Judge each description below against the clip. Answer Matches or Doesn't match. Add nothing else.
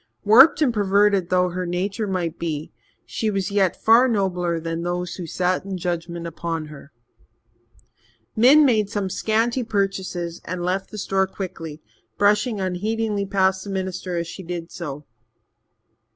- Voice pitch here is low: Doesn't match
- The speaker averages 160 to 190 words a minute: Doesn't match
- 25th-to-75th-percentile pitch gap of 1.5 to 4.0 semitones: Matches